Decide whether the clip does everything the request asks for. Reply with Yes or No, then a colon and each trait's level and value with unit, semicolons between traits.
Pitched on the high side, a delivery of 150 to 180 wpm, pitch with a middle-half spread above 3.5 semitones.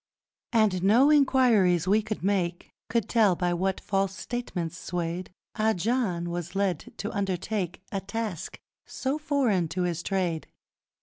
No: high, 195 Hz; average, 140 wpm; average, 4.0 semitones